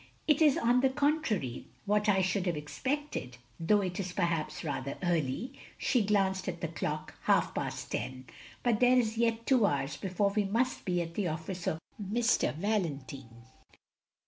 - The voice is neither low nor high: No, high, 195 Hz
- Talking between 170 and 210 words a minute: Yes, average, 175 wpm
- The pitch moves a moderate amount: No, wide, 6.3 semitones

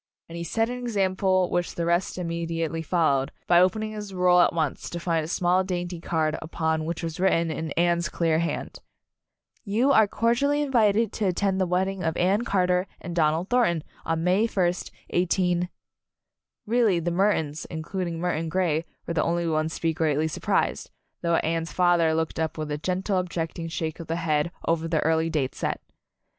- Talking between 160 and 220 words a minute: Yes, average, 185 wpm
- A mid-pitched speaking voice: Yes, medium, 170 Hz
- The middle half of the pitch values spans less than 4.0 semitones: Yes, narrow, 2.5 semitones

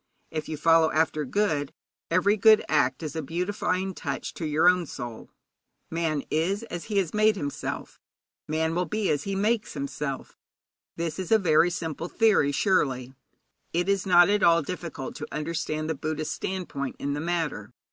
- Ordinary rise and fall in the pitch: Yes, average, 3.7 semitones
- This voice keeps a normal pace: Yes, average, 170 wpm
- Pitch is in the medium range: Yes, medium, 165 Hz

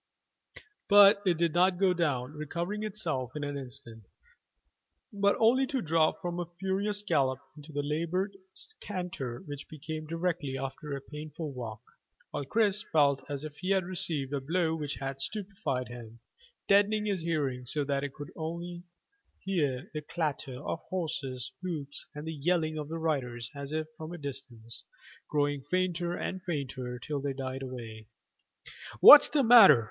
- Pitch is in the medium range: Yes, medium, 155 Hz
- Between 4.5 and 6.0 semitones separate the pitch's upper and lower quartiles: Yes, average, 4.8 semitones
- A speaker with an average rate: Yes, average, 160 wpm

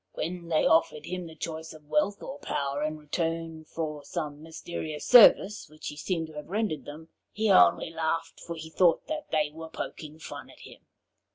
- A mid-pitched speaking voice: Yes, medium, 160 Hz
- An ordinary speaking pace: Yes, average, 190 wpm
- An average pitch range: No, narrow, 2.0 semitones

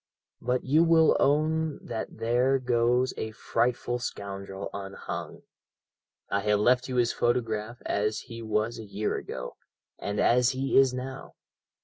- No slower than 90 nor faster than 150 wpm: Yes, average, 140 wpm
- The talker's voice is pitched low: Yes, low, 120 Hz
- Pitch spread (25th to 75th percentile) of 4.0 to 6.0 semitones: No, average, 3.3 semitones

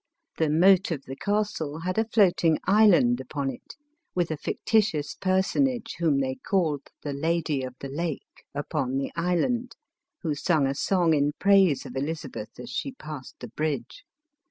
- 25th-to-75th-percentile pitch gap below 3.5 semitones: No, average, 5.3 semitones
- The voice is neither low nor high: Yes, medium, 160 Hz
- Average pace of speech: Yes, average, 160 wpm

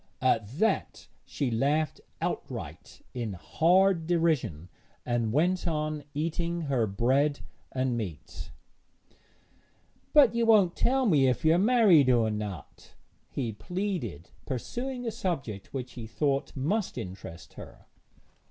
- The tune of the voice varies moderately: No, wide, 7.3 semitones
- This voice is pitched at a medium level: Yes, medium, 145 Hz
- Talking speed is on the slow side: Yes, slow, 125 wpm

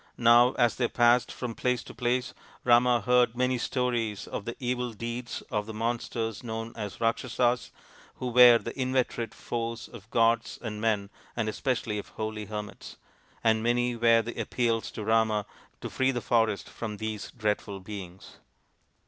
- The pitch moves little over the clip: Yes, narrow, 1.9 semitones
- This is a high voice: No, low, 115 Hz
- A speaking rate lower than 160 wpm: No, average, 165 wpm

